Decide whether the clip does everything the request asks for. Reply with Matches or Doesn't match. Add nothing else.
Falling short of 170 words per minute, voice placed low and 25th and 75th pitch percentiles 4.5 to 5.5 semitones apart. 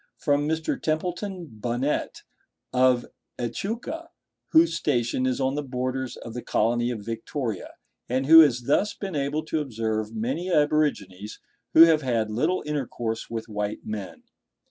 Matches